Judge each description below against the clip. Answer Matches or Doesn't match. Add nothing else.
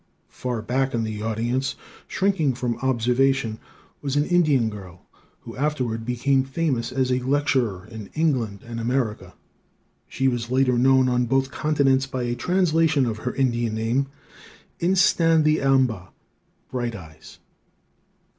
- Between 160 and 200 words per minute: Doesn't match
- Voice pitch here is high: Doesn't match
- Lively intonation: Doesn't match